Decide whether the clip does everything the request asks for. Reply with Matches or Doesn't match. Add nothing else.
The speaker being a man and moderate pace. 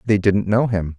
Doesn't match